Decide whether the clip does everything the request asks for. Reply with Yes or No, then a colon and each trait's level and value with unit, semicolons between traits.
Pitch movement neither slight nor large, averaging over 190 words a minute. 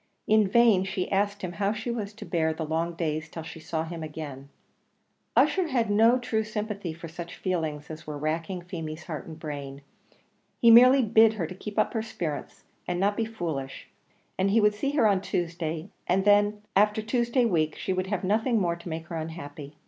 Yes: average, 5.0 semitones; average, 200 wpm